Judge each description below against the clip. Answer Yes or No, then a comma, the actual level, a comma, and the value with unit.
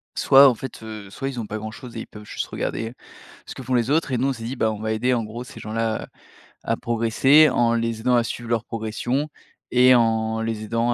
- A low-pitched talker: Yes, low, 115 Hz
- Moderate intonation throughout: No, narrow, 2.3 semitones